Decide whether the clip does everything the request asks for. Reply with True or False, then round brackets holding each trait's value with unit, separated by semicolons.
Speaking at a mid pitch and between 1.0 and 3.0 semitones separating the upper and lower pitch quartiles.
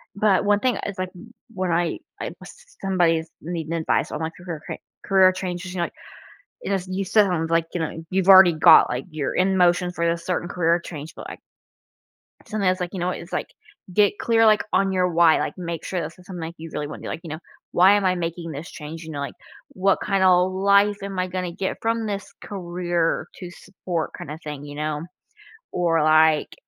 True (180 Hz; 2.7 semitones)